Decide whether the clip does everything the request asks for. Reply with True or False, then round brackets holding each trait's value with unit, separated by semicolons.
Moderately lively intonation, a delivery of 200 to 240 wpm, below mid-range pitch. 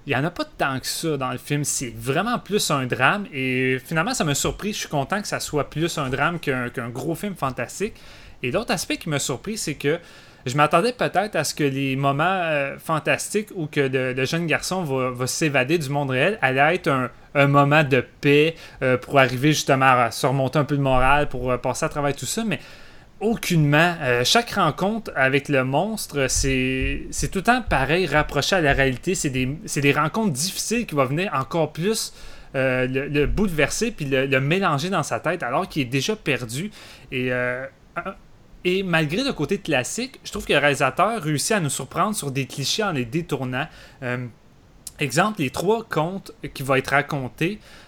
False (4.6 semitones; 210 wpm; 145 Hz)